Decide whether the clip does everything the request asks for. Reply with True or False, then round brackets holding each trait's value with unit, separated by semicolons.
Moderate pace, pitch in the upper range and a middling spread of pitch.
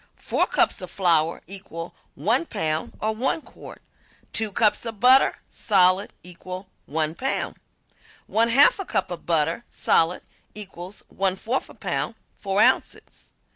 False (130 wpm; 195 Hz; 4.5 semitones)